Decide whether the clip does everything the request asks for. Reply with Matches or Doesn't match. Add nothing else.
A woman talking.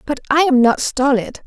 Matches